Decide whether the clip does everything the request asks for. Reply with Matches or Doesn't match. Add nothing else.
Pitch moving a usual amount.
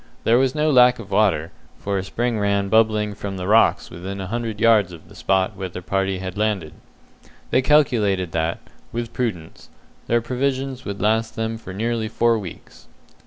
Matches